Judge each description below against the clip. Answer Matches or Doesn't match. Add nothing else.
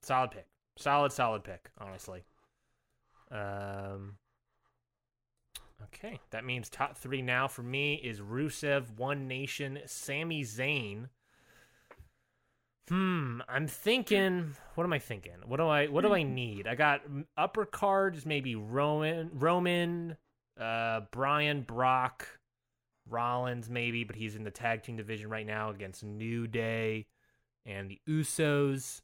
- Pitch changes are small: Doesn't match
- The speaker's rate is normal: Doesn't match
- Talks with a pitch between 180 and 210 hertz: Doesn't match